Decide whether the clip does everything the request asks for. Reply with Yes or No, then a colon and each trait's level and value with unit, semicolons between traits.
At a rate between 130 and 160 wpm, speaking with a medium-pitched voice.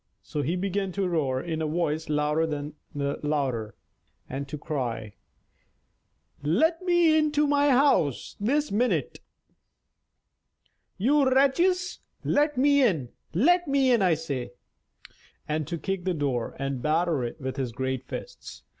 Yes: average, 140 wpm; medium, 165 Hz